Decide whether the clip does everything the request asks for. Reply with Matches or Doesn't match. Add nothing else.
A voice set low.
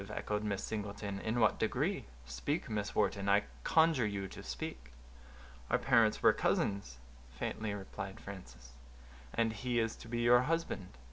Matches